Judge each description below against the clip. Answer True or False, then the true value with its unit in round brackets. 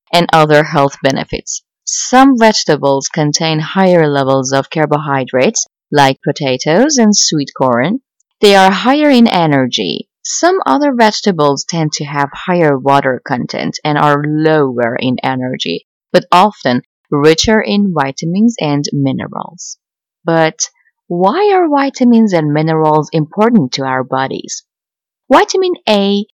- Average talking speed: True (125 wpm)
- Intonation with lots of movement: True (7.6 semitones)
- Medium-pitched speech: True (160 Hz)